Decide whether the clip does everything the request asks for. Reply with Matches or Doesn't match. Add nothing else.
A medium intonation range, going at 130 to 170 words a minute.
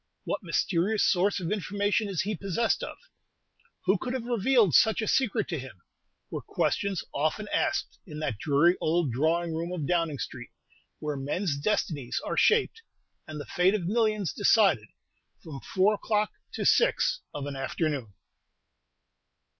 Doesn't match